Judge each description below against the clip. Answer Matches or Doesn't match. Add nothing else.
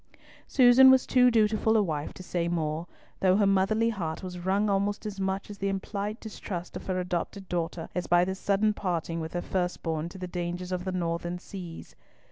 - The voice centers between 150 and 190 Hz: Matches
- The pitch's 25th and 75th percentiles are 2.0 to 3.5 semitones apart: Matches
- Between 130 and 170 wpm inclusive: Doesn't match